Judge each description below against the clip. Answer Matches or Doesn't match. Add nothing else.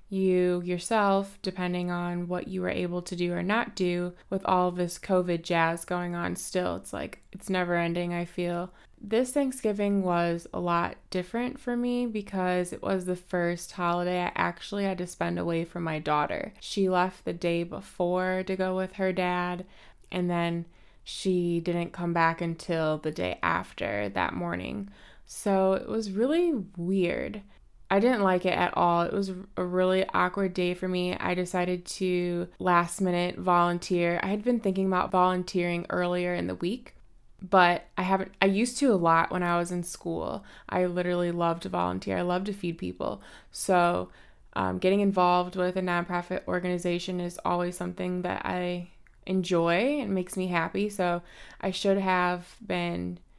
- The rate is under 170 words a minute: Doesn't match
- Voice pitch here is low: Doesn't match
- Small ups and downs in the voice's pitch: Matches